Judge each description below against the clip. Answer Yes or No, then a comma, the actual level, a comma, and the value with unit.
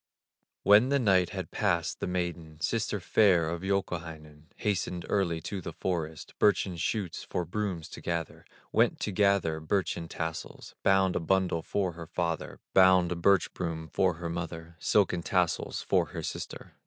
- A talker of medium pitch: No, very low, 90 Hz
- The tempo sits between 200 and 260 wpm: No, average, 160 wpm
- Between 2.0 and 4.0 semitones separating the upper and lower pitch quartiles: Yes, average, 2.7 semitones